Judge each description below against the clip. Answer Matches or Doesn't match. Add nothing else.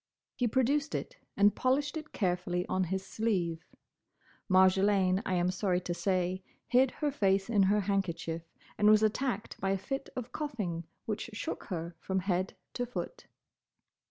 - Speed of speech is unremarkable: Matches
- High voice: Matches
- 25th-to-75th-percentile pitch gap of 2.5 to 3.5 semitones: Doesn't match